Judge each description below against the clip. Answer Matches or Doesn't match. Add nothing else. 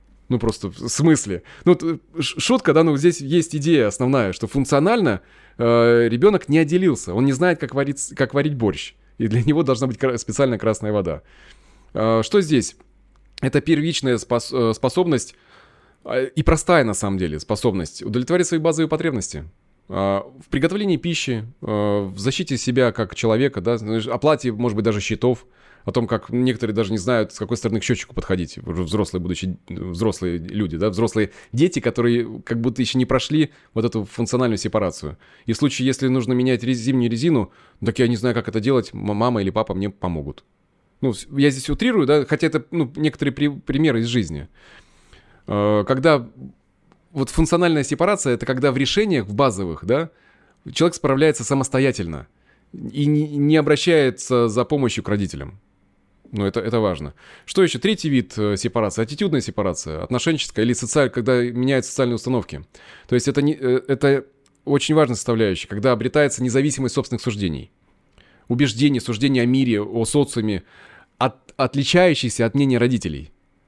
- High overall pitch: Doesn't match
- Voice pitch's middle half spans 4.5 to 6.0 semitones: Matches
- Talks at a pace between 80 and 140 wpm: Doesn't match